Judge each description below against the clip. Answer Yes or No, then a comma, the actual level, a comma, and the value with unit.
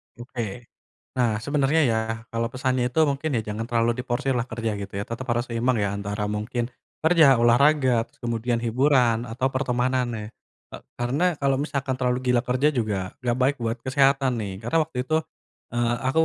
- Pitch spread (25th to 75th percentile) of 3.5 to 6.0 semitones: No, narrow, 2.5 semitones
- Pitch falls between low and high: No, low, 125 Hz